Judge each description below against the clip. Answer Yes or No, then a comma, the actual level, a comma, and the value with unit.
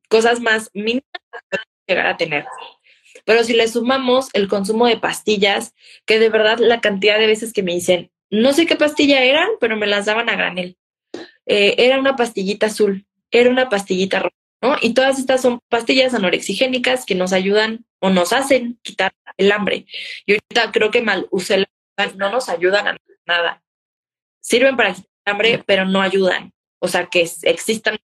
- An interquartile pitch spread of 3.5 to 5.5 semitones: Yes, average, 4.2 semitones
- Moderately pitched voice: No, high, 220 Hz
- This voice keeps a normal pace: Yes, average, 180 wpm